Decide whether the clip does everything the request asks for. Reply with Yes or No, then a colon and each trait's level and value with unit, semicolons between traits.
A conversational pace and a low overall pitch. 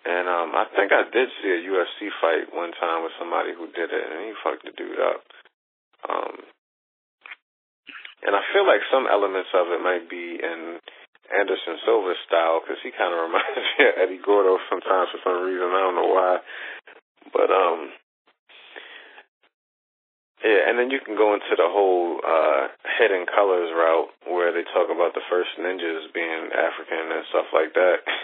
Yes: average, 180 wpm; low, 100 Hz